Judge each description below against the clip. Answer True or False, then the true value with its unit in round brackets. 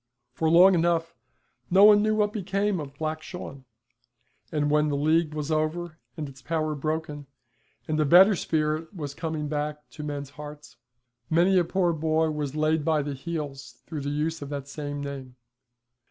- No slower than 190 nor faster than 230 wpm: False (175 wpm)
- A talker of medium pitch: True (155 Hz)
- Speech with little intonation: True (2.3 semitones)